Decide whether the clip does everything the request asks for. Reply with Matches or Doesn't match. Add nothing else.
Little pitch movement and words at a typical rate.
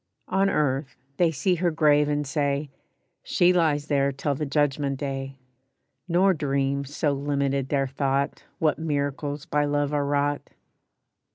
Matches